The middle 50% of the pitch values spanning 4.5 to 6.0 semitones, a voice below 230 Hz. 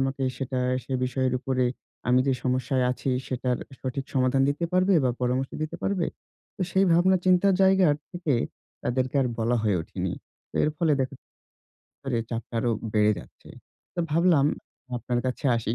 Yes: average, 4.9 semitones; low, 135 Hz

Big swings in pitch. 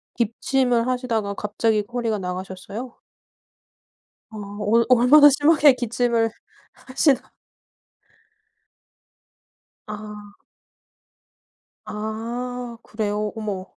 No: average, 2.9 semitones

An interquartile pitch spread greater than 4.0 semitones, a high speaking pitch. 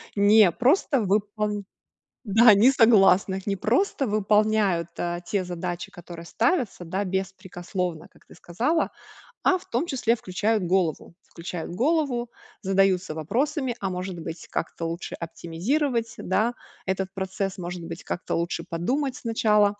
Yes: average, 4.5 semitones; high, 195 Hz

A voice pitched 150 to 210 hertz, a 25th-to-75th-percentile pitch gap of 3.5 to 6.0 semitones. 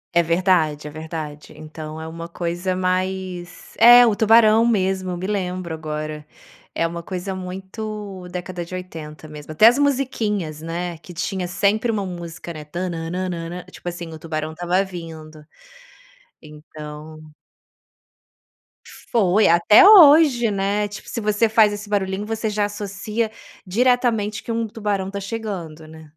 Yes: medium, 185 Hz; average, 4.2 semitones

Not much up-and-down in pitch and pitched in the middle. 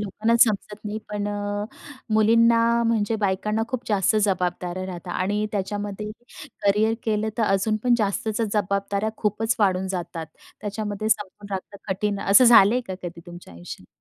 No: narrow, 2.1 semitones; high, 205 Hz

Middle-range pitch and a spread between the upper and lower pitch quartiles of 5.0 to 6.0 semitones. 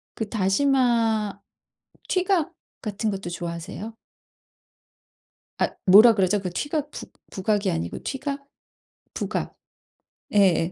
No: high, 210 Hz; average, 5.3 semitones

